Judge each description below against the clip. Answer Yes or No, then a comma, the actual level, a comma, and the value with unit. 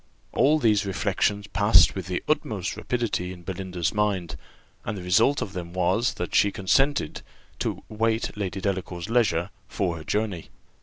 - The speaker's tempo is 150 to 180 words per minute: Yes, average, 155 wpm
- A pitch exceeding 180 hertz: No, low, 100 Hz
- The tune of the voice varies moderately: Yes, average, 3.5 semitones